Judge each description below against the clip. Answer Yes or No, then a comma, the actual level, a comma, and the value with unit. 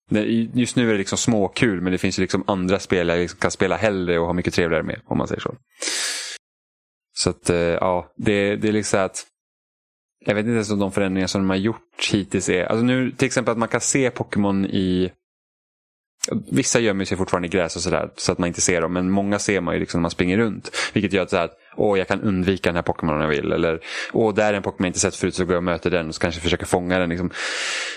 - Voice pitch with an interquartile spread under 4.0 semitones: Yes, average, 3.1 semitones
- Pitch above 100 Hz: No, very low, 95 Hz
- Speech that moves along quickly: Yes, fast, 260 wpm